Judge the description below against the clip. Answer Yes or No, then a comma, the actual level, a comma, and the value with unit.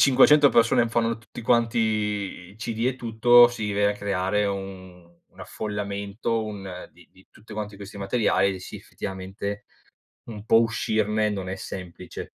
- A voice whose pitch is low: Yes, low, 105 Hz